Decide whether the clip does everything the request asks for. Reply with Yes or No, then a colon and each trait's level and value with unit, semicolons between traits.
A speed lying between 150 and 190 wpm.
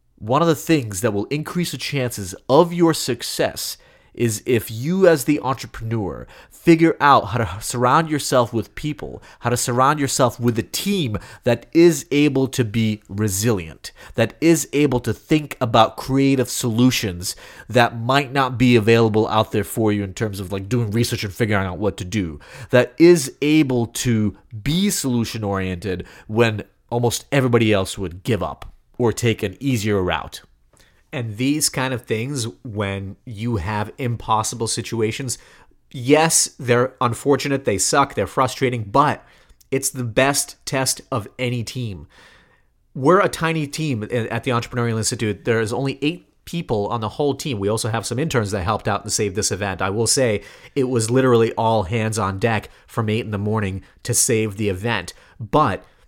Yes: average, 170 wpm